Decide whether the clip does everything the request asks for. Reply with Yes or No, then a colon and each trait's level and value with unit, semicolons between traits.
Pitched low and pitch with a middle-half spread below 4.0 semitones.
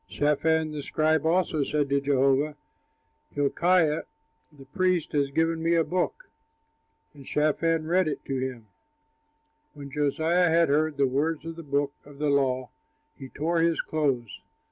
No: medium, 150 Hz; average, 2.7 semitones